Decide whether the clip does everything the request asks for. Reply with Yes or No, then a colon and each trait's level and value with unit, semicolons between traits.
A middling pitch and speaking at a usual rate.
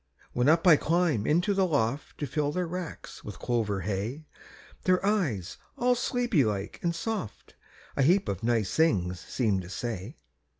Yes: medium, 145 Hz; average, 165 wpm